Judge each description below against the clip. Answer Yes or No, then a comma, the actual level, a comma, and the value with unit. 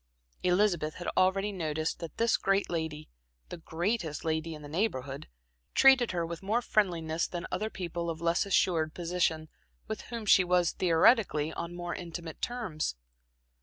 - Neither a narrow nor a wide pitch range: Yes, average, 3.4 semitones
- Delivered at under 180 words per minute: Yes, average, 155 wpm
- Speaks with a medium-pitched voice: Yes, medium, 175 Hz